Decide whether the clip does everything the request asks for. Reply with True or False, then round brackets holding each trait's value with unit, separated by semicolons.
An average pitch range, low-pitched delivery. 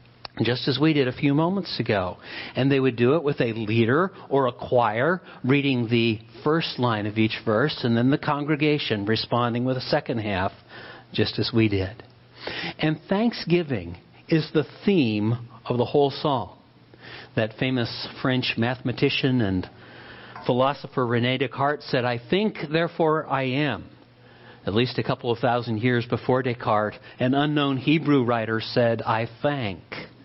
True (4.0 semitones; 125 Hz)